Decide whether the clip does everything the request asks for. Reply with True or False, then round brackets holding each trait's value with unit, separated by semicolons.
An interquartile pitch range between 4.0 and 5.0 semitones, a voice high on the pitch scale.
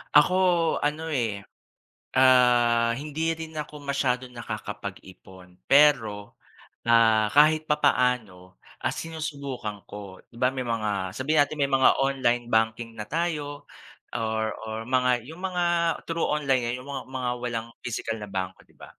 False (4.6 semitones; 125 Hz)